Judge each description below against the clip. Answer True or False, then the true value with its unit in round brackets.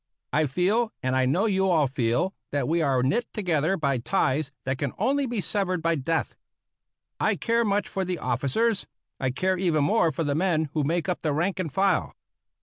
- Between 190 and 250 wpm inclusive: True (200 wpm)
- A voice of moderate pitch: True (165 Hz)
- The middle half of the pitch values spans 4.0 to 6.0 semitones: True (5.4 semitones)